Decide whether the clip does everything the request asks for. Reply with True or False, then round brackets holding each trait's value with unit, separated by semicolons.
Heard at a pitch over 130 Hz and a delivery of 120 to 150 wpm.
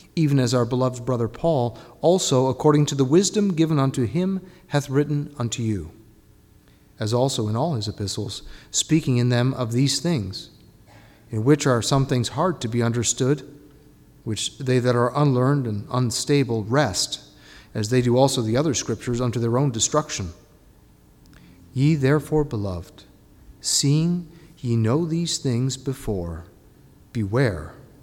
False (125 Hz; 145 wpm)